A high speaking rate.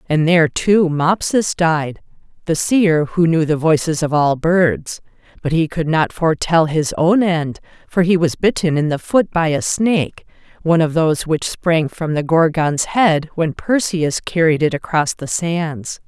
No: average, 180 wpm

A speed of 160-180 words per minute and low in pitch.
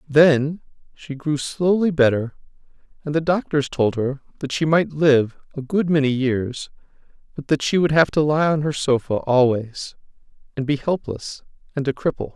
No: average, 170 wpm; medium, 145 Hz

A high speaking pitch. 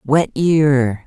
No: medium, 140 Hz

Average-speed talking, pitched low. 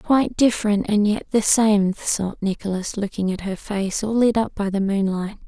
No: average, 195 wpm; high, 205 Hz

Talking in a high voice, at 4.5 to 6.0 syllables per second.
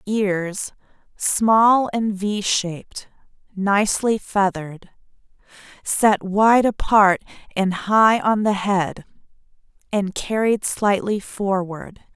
No: high, 200 Hz; 3.1 syllables/s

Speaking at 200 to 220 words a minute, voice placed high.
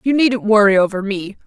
Yes: fast, 205 wpm; high, 210 Hz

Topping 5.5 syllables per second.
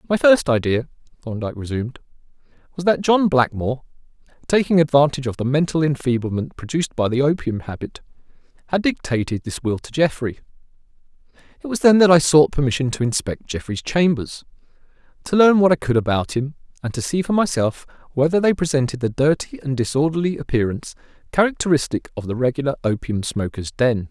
Yes: 6.0 syllables/s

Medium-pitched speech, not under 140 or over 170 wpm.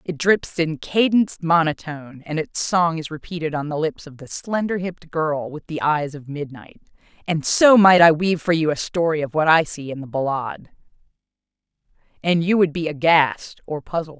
No: medium, 160 Hz; average, 190 wpm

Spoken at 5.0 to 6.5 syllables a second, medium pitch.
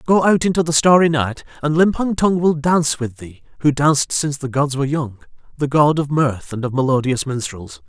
Yes: 5.5 syllables/s; medium, 145 Hz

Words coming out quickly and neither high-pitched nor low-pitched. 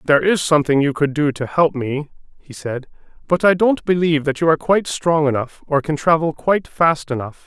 Yes: fast, 215 wpm; medium, 155 Hz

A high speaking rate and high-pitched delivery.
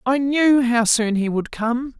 Yes: fast, 210 wpm; high, 245 Hz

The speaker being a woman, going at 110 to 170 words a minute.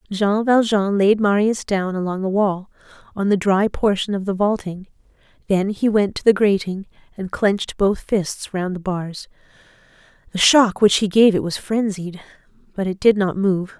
No: female; average, 180 wpm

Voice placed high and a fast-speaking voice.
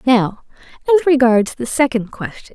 No: very high, 255 Hz; average, 140 wpm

